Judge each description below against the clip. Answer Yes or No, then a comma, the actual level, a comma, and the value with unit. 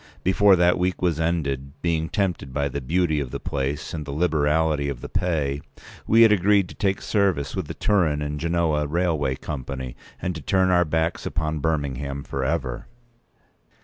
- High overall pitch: No, very low, 80 Hz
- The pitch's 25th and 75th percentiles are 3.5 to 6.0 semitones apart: Yes, average, 3.9 semitones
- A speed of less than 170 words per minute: No, average, 180 wpm